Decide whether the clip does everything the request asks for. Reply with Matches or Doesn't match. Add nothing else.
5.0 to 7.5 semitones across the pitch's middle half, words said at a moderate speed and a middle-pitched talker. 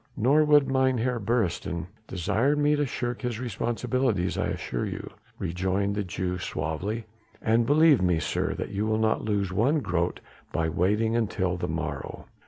Doesn't match